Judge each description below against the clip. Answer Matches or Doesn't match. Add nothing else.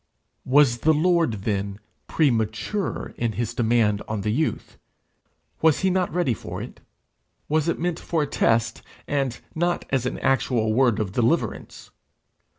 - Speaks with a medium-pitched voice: Doesn't match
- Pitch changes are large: Matches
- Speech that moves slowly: Doesn't match